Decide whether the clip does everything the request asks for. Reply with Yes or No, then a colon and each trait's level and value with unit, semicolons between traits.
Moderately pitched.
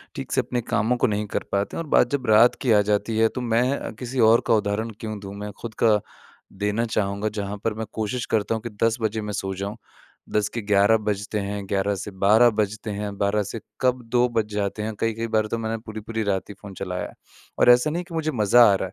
No: low, 110 Hz